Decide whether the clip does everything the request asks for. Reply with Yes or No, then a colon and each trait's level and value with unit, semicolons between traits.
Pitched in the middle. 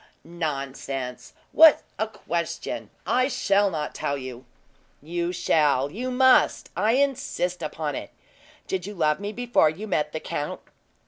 Yes: medium, 175 Hz